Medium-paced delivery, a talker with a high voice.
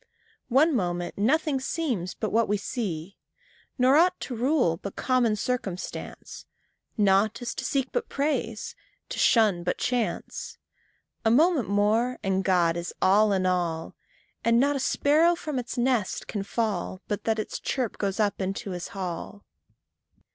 Yes: average, 160 wpm; high, 220 Hz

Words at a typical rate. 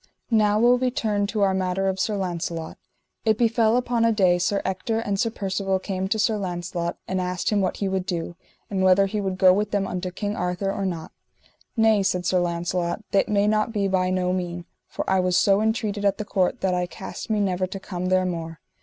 No: fast, 225 wpm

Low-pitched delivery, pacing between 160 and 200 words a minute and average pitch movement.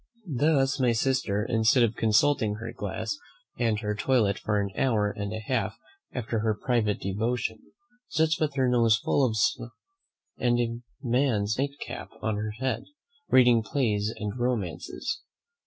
No: low, 115 Hz; average, 150 wpm; average, 3.3 semitones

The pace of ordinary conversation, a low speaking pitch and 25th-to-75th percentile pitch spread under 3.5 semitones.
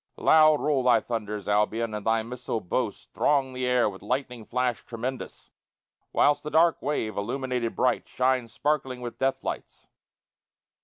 Yes: average, 150 wpm; low, 125 Hz; average, 2.8 semitones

